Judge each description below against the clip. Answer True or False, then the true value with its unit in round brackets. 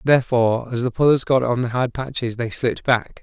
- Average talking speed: False (225 wpm)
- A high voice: False (125 Hz)